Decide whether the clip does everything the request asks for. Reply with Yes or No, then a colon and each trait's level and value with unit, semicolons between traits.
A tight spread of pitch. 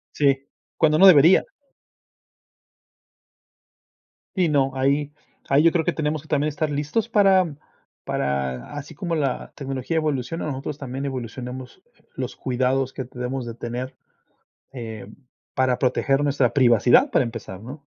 No: average, 3.3 semitones